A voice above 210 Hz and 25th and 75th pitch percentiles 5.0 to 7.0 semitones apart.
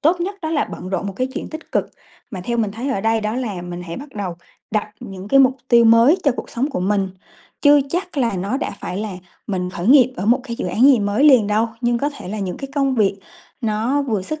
Yes: high, 230 Hz; wide, 5.5 semitones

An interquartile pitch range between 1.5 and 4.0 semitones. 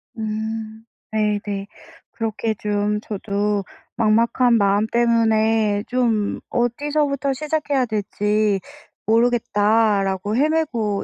Yes: narrow, 2.4 semitones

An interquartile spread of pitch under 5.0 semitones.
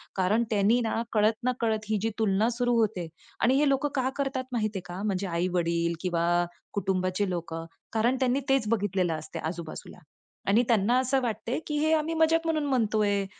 No: wide, 5.4 semitones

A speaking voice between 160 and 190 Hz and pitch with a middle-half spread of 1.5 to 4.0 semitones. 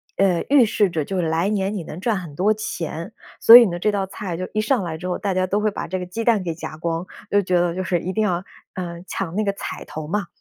Yes: medium, 185 Hz; average, 3.3 semitones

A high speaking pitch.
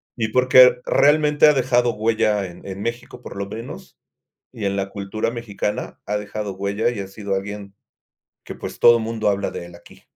No: low, 105 Hz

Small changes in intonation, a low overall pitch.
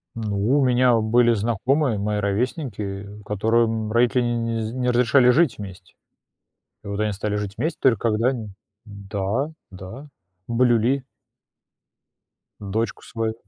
No: average, 3.2 semitones; low, 115 Hz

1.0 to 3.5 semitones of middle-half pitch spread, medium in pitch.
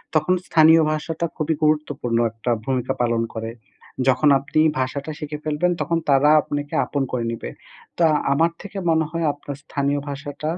Yes: average, 2.9 semitones; medium, 145 Hz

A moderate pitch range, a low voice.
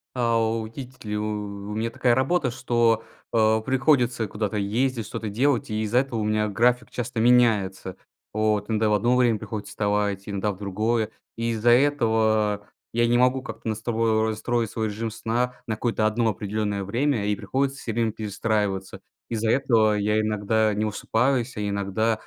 No: narrow, 2.2 semitones; low, 110 Hz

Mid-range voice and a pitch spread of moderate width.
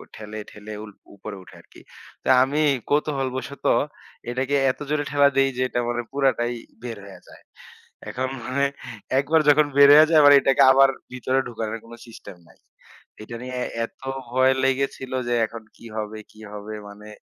No: low, 130 Hz; average, 3.9 semitones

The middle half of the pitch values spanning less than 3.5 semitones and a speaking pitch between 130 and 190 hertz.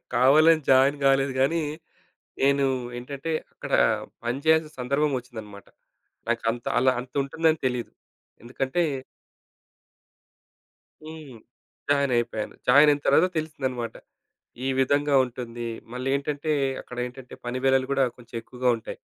Yes: average, 2.8 semitones; low, 135 Hz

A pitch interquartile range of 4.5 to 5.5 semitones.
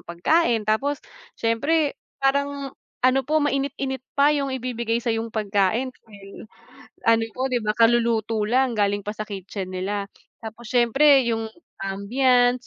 No: average, 3.9 semitones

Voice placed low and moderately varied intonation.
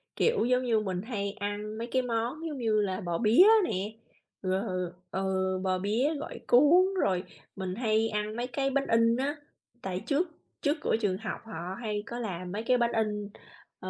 No: high, 220 Hz; average, 4.3 semitones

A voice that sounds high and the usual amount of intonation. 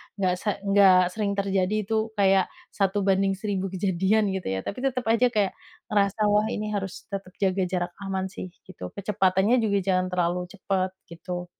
No: high, 195 Hz; narrow, 1.8 semitones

